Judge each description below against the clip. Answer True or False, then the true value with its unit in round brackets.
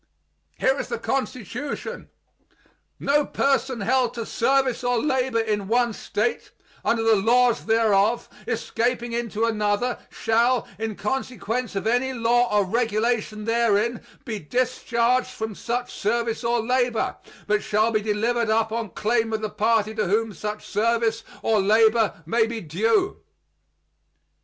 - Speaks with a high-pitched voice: True (230 Hz)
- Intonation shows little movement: True (2.1 semitones)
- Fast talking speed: False (135 wpm)